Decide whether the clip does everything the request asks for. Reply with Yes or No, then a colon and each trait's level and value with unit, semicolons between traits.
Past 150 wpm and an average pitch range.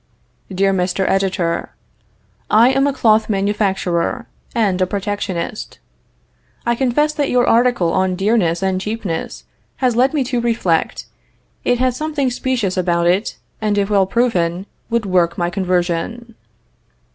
No: slow, 135 wpm; average, 4.6 semitones